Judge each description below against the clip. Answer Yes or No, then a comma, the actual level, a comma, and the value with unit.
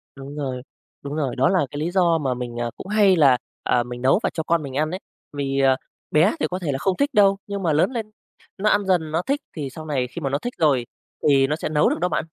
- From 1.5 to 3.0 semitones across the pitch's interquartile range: No, wide, 5.4 semitones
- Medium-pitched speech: Yes, medium, 155 Hz